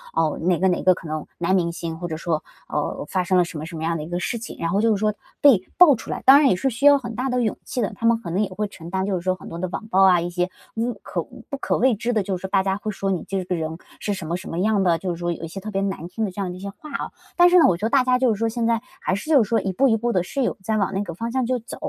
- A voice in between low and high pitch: No, high, 195 Hz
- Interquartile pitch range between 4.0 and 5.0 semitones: Yes, average, 4.7 semitones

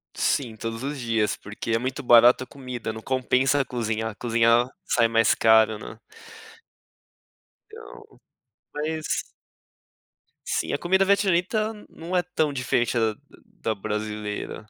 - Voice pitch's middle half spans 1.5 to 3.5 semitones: No, average, 4.7 semitones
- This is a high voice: No, low, 120 Hz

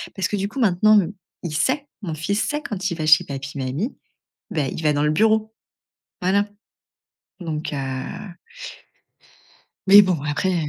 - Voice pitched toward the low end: No, medium, 175 Hz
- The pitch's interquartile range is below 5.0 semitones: No, average, 5.3 semitones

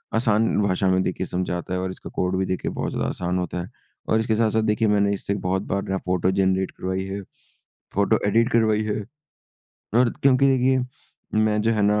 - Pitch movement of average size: Yes, average, 3.0 semitones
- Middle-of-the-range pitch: No, low, 100 Hz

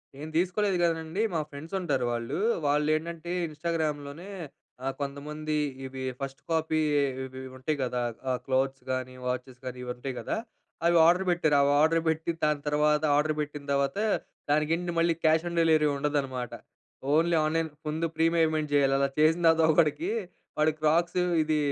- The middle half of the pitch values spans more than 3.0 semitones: No, average, 2.7 semitones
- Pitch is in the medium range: Yes, medium, 155 Hz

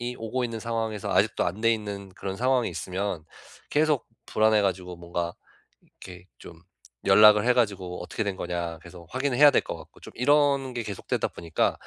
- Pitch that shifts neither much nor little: Yes, average, 5.0 semitones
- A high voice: No, low, 105 Hz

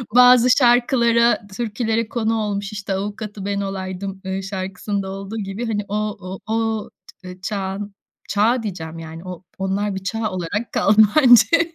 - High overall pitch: Yes, high, 205 Hz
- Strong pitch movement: No, average, 2.8 semitones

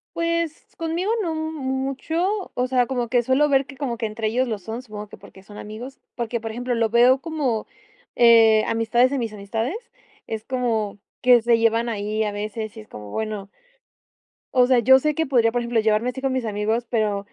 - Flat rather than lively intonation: No, average, 3.2 semitones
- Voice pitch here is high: Yes, high, 235 Hz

